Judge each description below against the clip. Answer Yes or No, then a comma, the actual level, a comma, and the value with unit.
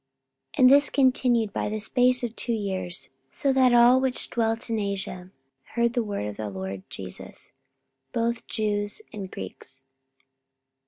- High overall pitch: Yes, high, 225 Hz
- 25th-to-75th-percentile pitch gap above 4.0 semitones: Yes, average, 4.6 semitones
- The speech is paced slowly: No, average, 160 wpm